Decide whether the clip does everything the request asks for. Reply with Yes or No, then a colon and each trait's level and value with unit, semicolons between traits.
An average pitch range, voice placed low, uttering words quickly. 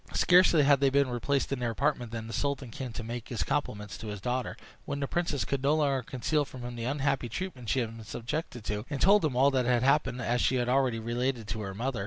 Yes: average, 3.2 semitones; low, 130 Hz; fast, 260 wpm